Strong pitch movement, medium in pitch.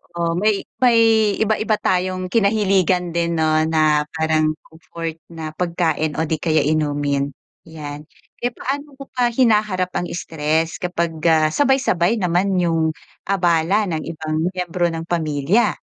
No: average, 3.6 semitones; medium, 170 Hz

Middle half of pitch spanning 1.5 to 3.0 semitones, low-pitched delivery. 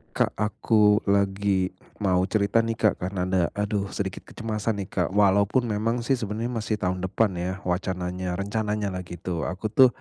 Yes: narrow, 2.6 semitones; low, 100 Hz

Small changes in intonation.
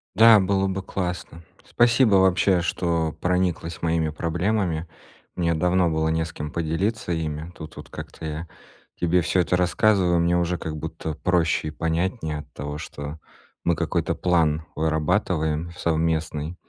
Yes: narrow, 2.3 semitones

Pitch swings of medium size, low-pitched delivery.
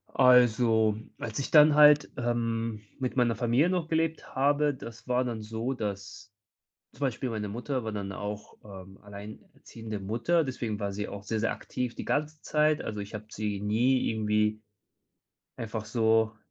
Yes: average, 3.5 semitones; low, 115 Hz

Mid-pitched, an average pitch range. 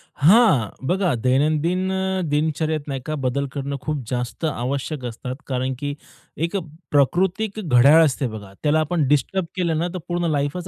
Yes: medium, 150 Hz; average, 4.6 semitones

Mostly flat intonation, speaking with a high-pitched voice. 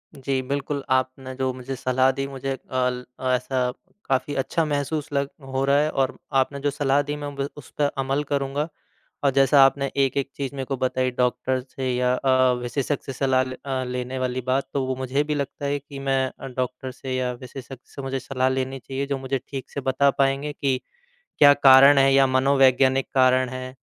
No: narrow, 1.2 semitones; low, 135 Hz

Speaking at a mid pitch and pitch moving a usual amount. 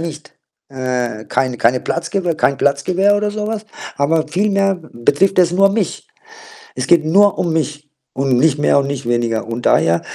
No: medium, 155 Hz; wide, 6.7 semitones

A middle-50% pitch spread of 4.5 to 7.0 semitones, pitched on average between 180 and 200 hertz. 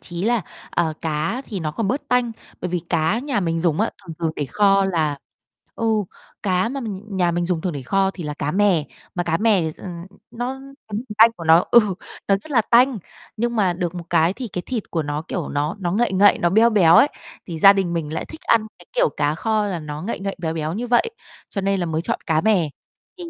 Yes: average, 5.1 semitones; high, 190 Hz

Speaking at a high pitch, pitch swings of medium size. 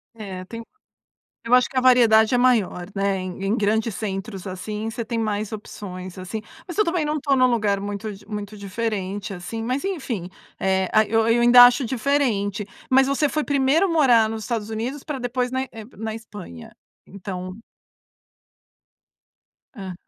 Yes: high, 220 Hz; average, 3.9 semitones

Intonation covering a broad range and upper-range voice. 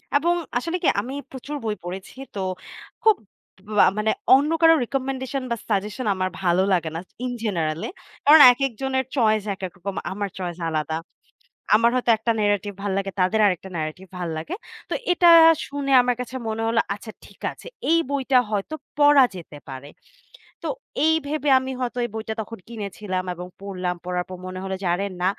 Yes: wide, 6.1 semitones; high, 215 Hz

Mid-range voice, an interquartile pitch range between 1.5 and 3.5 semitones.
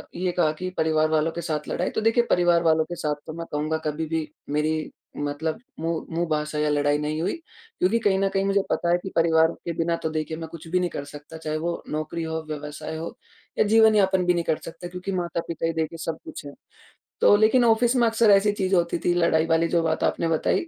Yes: medium, 165 Hz; narrow, 2.6 semitones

